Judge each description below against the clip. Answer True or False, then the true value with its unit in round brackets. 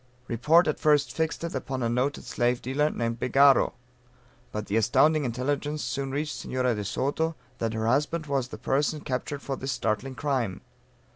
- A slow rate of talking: False (170 wpm)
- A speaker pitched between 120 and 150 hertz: True (135 Hz)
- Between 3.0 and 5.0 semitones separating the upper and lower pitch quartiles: True (3.5 semitones)